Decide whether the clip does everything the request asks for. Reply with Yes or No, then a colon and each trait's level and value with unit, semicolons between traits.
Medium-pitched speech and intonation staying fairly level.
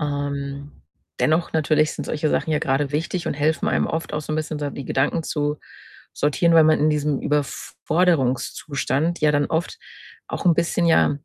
Yes: medium, 150 Hz; narrow, 1.9 semitones